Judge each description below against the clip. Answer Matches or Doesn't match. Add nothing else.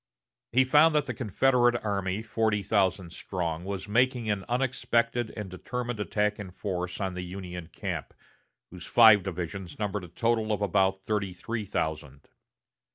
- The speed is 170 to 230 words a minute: Doesn't match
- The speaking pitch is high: Doesn't match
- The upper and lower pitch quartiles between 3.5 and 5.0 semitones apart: Matches